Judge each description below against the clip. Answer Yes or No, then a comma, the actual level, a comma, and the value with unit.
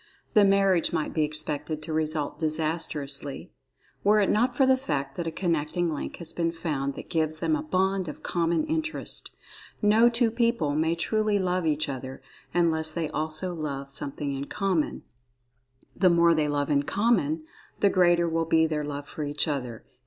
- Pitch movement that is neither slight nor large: Yes, average, 4.0 semitones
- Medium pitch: Yes, medium, 160 Hz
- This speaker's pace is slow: No, average, 175 wpm